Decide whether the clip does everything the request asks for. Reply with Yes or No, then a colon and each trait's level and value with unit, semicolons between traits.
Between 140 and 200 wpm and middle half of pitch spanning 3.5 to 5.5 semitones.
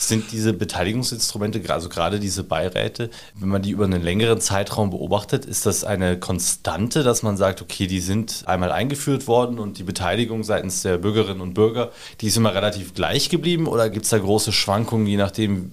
No: fast, 190 wpm; average, 2.9 semitones